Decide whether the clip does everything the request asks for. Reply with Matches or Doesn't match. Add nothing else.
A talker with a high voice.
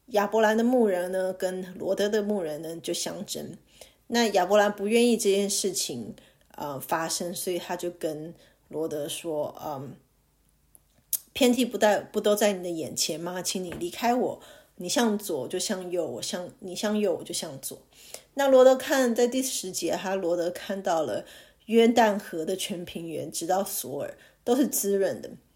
Matches